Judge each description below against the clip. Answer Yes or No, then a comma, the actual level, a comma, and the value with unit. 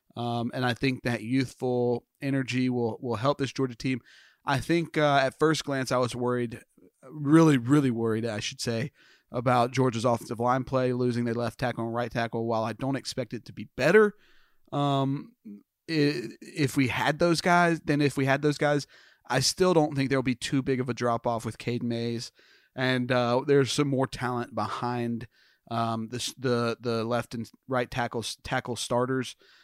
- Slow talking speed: No, average, 185 wpm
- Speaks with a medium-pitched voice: No, low, 125 Hz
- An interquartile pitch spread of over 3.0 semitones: No, average, 2.7 semitones